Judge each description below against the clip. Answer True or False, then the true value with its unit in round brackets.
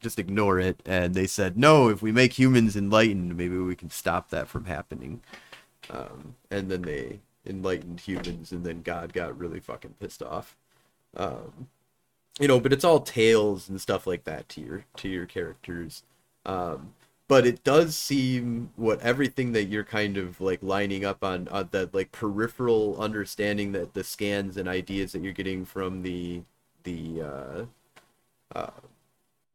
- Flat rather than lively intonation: False (3.4 semitones)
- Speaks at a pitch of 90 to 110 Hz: True (100 Hz)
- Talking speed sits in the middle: True (165 wpm)